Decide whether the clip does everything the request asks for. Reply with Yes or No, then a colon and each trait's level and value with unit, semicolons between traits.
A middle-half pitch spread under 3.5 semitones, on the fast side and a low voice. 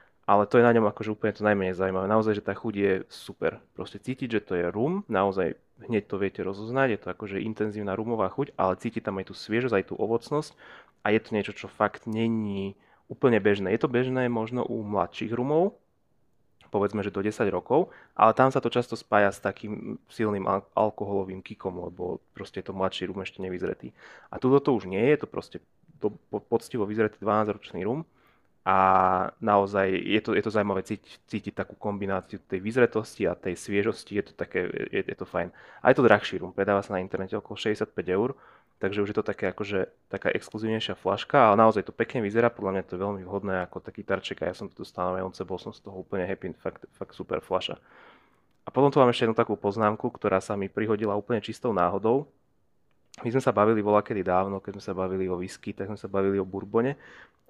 Yes: narrow, 2.6 semitones; fast, 210 wpm; low, 105 Hz